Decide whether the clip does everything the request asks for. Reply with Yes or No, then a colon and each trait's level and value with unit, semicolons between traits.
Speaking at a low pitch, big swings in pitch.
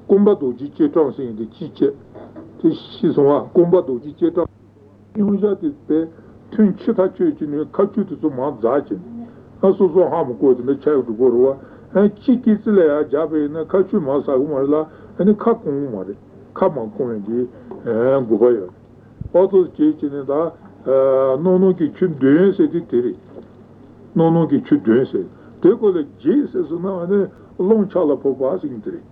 No: medium, 175 Hz; wide, 7.5 semitones